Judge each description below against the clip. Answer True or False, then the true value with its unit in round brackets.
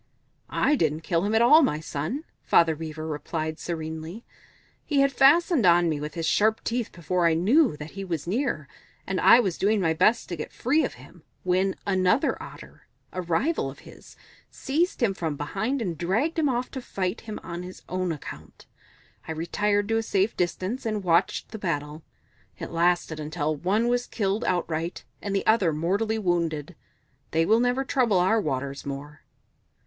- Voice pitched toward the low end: False (185 Hz)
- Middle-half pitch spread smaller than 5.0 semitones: False (5.6 semitones)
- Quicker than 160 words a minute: True (180 wpm)